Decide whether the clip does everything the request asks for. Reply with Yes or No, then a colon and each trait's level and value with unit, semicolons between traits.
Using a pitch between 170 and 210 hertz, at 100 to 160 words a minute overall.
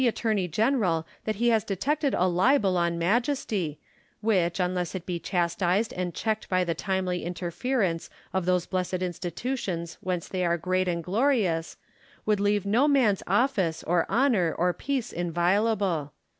Yes: medium, 185 Hz; average, 150 wpm